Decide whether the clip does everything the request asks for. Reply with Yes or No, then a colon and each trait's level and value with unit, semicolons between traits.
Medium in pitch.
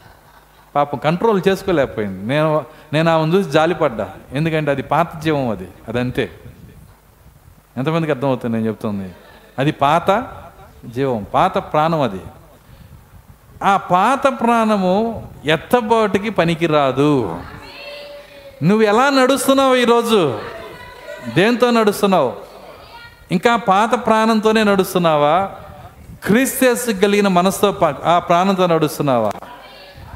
Yes: medium, 175 Hz